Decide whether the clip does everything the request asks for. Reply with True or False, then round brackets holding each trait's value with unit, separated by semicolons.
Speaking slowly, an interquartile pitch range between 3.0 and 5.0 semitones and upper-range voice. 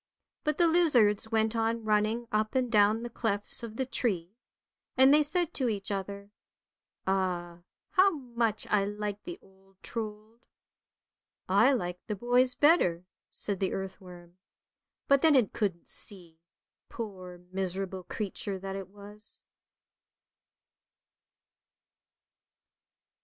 True (125 wpm; 3.9 semitones; 210 Hz)